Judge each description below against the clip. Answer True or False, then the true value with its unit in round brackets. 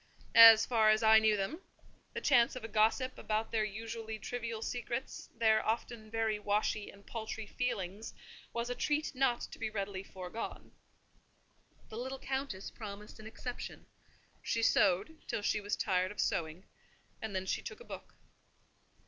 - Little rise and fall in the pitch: True (2.1 semitones)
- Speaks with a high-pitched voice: True (220 Hz)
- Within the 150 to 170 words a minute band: True (160 wpm)